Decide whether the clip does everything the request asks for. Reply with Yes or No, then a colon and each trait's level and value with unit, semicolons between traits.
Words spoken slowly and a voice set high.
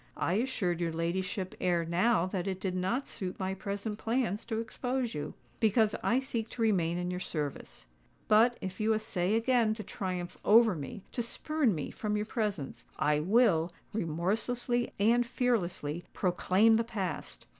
No: average, 155 wpm; high, 205 Hz